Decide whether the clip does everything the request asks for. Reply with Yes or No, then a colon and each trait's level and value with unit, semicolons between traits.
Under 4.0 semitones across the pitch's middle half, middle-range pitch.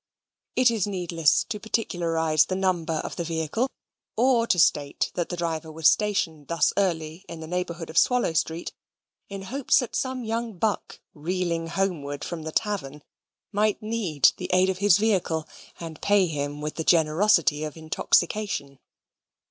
No: average, 4.4 semitones; medium, 170 Hz